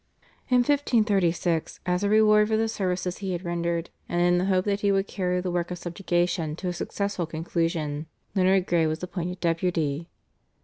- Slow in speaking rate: No, average, 180 wpm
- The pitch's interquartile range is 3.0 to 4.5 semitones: No, narrow, 2.6 semitones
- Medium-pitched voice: Yes, medium, 180 Hz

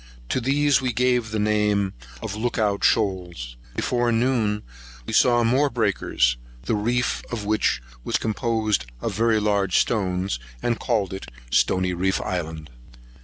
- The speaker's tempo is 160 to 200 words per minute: No, average, 145 wpm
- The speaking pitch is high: No, low, 105 Hz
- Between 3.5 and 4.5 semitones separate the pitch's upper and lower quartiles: Yes, average, 4.0 semitones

